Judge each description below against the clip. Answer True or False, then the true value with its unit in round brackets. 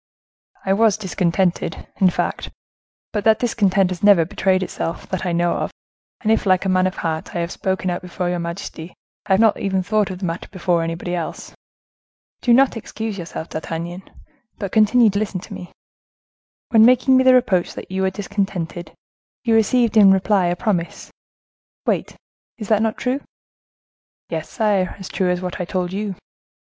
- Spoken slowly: False (180 wpm)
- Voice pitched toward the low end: False (190 Hz)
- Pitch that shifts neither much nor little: True (3.3 semitones)